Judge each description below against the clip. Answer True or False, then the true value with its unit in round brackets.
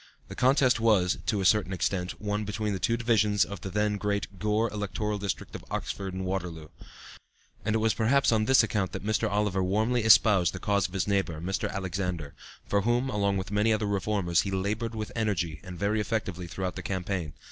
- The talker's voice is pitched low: True (100 Hz)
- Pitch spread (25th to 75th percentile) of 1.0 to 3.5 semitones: True (2.5 semitones)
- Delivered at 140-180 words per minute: False (200 wpm)